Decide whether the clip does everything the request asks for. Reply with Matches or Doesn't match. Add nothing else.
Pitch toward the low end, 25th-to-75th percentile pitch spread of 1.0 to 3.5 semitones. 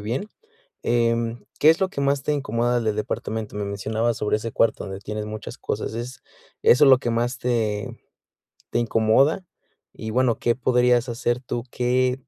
Matches